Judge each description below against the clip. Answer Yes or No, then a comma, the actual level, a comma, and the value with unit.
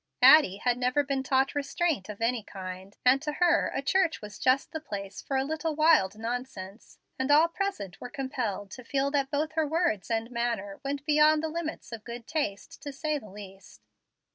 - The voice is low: No, very high, 265 Hz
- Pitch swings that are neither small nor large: No, wide, 6.1 semitones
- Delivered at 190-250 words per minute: Yes, average, 195 wpm